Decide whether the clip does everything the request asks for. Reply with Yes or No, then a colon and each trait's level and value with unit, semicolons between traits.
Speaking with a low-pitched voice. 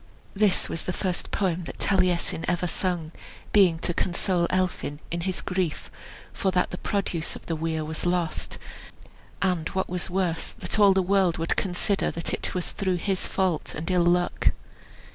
No: medium, 180 Hz